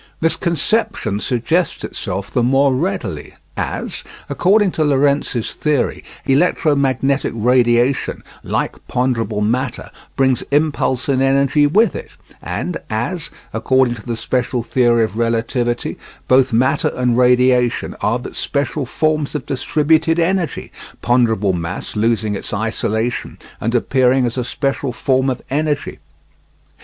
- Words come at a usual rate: No, slow, 125 wpm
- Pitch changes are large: No, average, 3.5 semitones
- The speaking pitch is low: Yes, low, 130 Hz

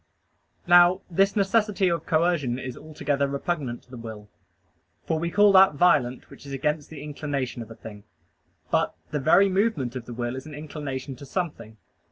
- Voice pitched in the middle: Yes, medium, 150 Hz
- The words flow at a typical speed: Yes, average, 180 wpm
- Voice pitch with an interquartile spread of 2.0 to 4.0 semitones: No, wide, 5.4 semitones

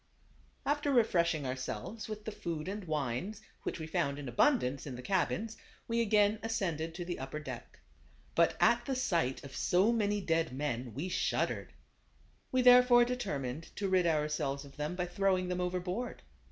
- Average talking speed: Yes, average, 175 wpm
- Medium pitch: Yes, medium, 180 Hz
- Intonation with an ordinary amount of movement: No, wide, 6.3 semitones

